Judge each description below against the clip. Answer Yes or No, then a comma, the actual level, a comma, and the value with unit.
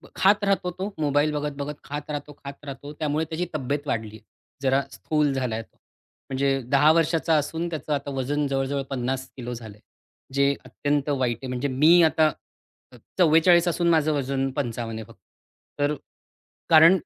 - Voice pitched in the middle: Yes, medium, 145 Hz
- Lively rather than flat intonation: No, average, 2.8 semitones